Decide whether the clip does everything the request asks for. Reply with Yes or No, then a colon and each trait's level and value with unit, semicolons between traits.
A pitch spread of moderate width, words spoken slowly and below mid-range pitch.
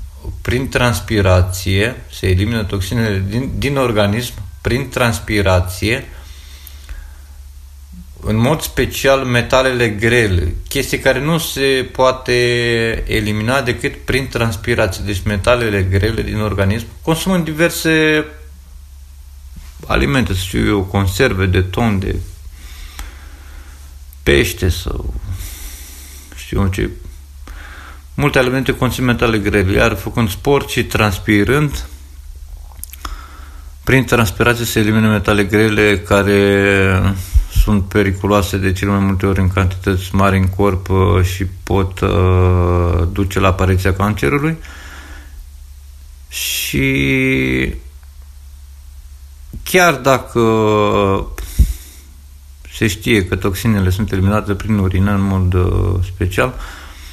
No: wide, 7.2 semitones; slow, 100 wpm; very low, 95 Hz